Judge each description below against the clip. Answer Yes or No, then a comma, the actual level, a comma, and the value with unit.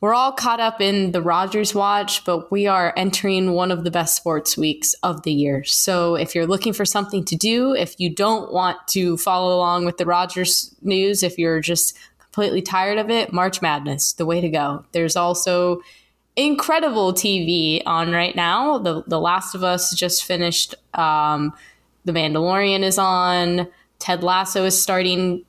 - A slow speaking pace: No, average, 175 wpm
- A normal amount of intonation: No, narrow, 2.2 semitones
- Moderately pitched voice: Yes, medium, 180 Hz